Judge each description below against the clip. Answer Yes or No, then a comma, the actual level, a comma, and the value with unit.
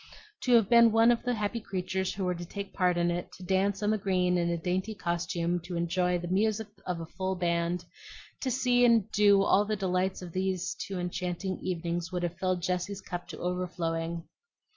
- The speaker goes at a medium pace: No, fast, 210 wpm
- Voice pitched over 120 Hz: Yes, medium, 185 Hz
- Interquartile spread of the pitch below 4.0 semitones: Yes, narrow, 2.4 semitones